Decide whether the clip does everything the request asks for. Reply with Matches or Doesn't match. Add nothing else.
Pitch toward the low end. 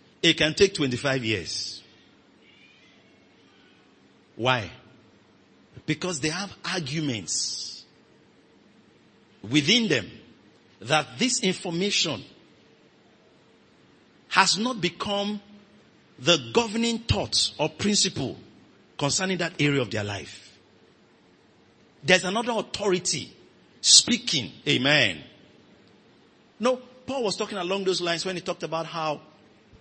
Doesn't match